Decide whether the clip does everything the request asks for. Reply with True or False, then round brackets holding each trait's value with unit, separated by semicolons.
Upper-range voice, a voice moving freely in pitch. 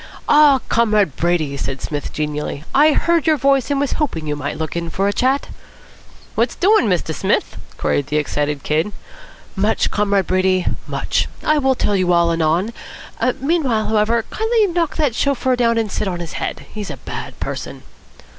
True (210 Hz; 8.8 semitones)